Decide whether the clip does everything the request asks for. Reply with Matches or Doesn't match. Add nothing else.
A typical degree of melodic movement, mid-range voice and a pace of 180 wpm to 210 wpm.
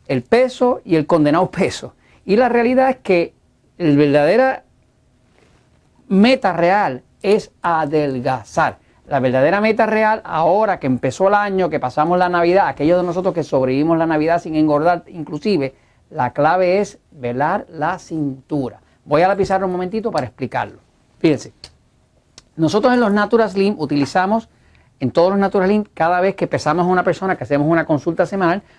Doesn't match